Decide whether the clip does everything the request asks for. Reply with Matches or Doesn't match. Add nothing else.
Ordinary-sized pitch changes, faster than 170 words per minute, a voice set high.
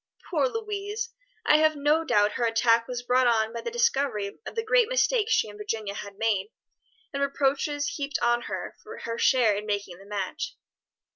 Doesn't match